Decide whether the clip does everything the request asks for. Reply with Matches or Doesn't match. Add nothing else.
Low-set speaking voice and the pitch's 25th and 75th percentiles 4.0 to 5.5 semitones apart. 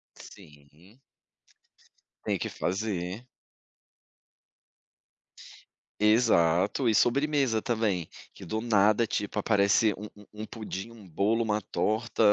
Doesn't match